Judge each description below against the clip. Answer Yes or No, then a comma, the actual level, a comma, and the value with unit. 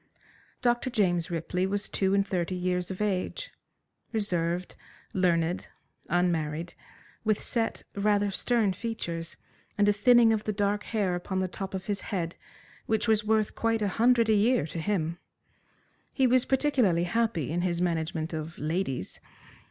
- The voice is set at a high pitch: Yes, high, 195 Hz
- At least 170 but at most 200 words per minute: No, average, 150 wpm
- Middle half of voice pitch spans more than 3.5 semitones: Yes, average, 4.1 semitones